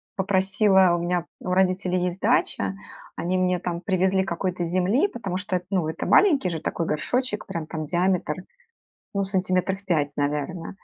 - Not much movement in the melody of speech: Yes, narrow, 1.8 semitones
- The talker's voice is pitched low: No, medium, 185 Hz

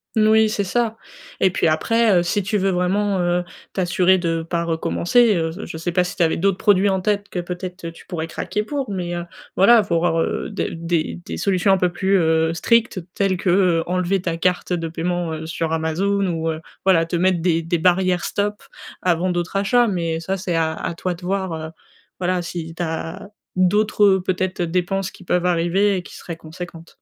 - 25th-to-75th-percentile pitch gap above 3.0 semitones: No, average, 2.7 semitones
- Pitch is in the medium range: Yes, medium, 180 Hz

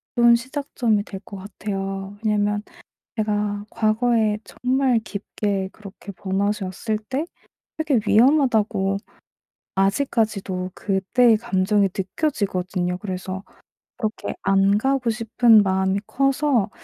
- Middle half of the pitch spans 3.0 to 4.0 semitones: Yes, average, 3.5 semitones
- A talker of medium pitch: No, high, 210 Hz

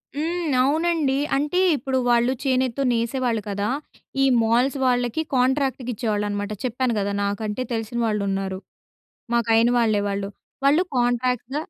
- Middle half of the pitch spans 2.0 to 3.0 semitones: No, average, 3.6 semitones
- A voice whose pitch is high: Yes, high, 245 Hz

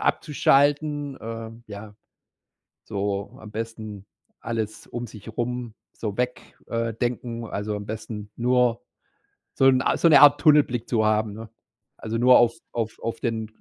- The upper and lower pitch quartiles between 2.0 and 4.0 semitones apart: Yes, narrow, 2.4 semitones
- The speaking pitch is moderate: No, low, 115 Hz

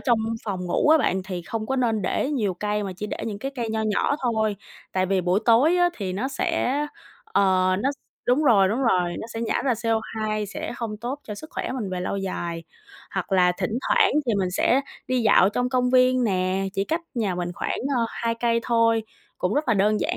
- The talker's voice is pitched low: No, high, 220 Hz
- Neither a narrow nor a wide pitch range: Yes, average, 4.5 semitones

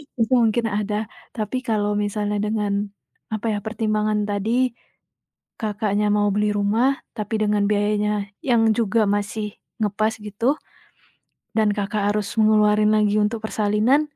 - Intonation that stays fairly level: Yes, narrow, 1.1 semitones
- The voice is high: Yes, high, 210 Hz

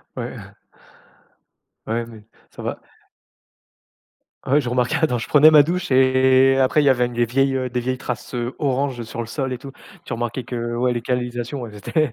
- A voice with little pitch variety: Yes, narrow, 2.1 semitones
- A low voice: Yes, low, 125 Hz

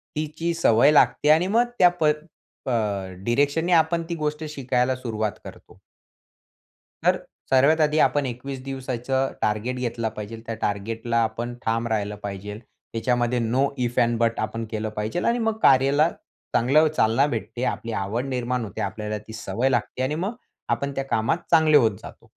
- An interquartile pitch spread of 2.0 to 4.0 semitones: No, average, 4.7 semitones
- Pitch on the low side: Yes, low, 125 Hz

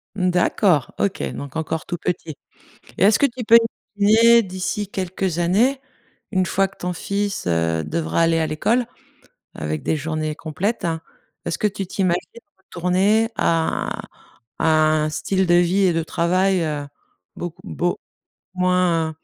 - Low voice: No, medium, 180 Hz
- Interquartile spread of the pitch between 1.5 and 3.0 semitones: No, average, 3.5 semitones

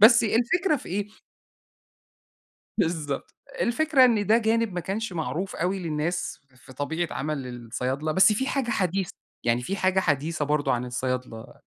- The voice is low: No, medium, 175 Hz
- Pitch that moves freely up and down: Yes, wide, 7.4 semitones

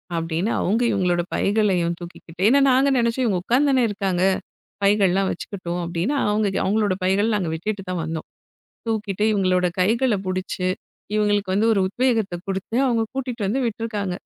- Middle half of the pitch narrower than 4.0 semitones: Yes, average, 3.6 semitones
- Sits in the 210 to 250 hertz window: No, high, 200 Hz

